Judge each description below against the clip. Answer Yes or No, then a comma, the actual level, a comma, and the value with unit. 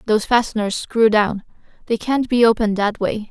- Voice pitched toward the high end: Yes, high, 220 Hz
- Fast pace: No, average, 180 wpm